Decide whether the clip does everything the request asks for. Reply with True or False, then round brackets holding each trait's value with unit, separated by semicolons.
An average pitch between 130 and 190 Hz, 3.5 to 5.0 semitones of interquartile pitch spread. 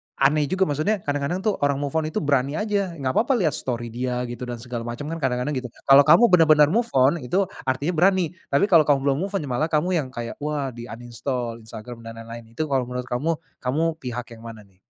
True (140 Hz; 4.5 semitones)